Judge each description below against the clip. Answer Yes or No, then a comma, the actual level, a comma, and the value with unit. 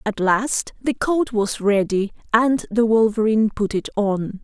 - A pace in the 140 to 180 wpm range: Yes, average, 160 wpm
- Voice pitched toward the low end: No, high, 220 Hz